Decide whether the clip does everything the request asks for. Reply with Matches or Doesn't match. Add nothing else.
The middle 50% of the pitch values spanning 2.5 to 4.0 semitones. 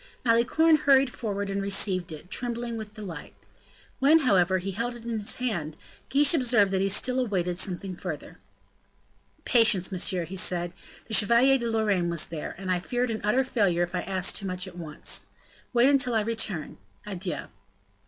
Doesn't match